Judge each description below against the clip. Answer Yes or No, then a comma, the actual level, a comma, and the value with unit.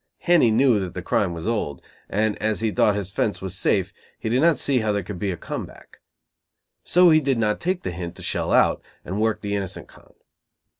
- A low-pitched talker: Yes, low, 105 Hz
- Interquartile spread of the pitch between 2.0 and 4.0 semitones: Yes, average, 3.6 semitones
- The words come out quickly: Yes, fast, 230 wpm